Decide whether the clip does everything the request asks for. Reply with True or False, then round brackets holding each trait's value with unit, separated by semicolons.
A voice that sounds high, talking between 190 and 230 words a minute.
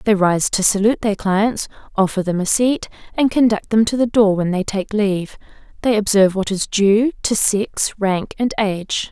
True (205 Hz; 200 wpm)